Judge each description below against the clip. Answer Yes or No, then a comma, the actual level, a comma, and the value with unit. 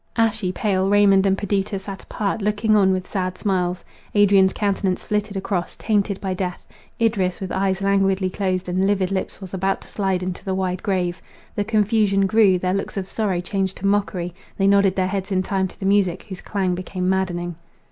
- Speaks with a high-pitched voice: Yes, high, 195 Hz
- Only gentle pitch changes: Yes, narrow, 1.5 semitones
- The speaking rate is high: No, average, 190 wpm